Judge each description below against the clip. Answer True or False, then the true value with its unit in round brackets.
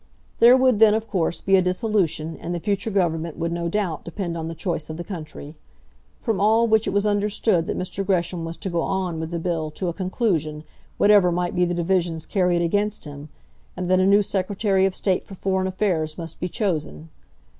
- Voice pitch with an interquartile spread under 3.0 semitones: False (3.4 semitones)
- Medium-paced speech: False (210 wpm)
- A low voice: False (180 Hz)